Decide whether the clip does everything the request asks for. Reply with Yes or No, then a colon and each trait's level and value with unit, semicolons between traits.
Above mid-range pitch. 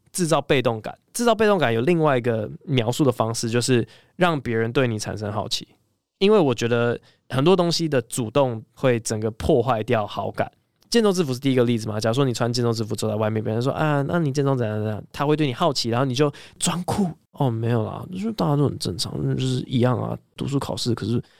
No: low, 125 Hz